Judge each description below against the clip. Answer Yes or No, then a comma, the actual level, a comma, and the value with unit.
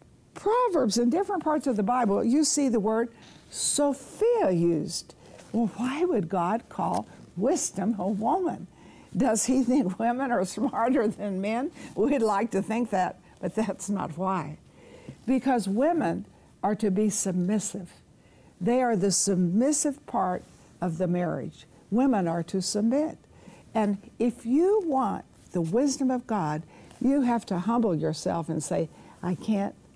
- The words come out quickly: No, average, 145 wpm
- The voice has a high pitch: Yes, high, 220 Hz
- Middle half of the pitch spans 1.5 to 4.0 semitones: No, wide, 5.5 semitones